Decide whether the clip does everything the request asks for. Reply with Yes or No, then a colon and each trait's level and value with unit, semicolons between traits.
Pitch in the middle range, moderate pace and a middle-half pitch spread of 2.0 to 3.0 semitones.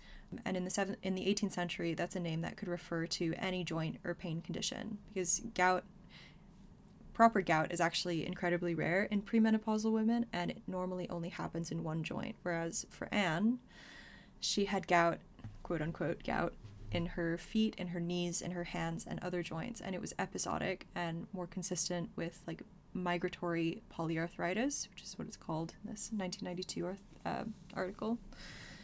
Yes: medium, 180 Hz; average, 170 wpm; average, 2.7 semitones